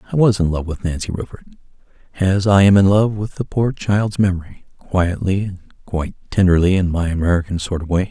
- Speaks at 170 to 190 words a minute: No, average, 200 wpm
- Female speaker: No, male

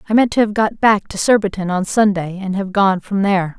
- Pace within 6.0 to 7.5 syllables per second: No, 5.6 syllables/s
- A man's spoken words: No, female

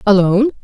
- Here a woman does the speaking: Yes, female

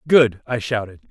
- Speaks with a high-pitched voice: No, low, 120 Hz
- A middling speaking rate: Yes, average, 165 wpm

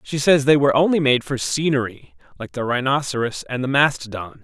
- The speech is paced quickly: No, average, 175 wpm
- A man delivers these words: Yes, male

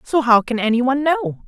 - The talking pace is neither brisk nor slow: No, fast, 245 wpm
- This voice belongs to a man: No, female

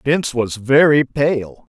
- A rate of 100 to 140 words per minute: Yes, slow, 135 wpm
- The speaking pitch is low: Yes, low, 130 Hz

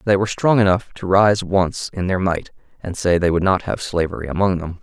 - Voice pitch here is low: Yes, very low, 95 Hz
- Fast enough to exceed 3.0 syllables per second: Yes, 5.5 syllables/s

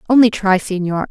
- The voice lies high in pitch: Yes, high, 200 Hz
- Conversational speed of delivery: Yes, average, 165 wpm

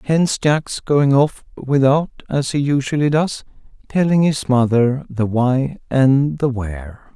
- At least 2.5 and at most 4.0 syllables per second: Yes, 3.9 syllables/s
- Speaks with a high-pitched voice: No, low, 135 Hz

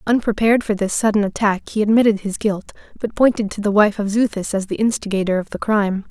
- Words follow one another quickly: Yes, fast, 215 wpm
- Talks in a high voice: Yes, high, 210 Hz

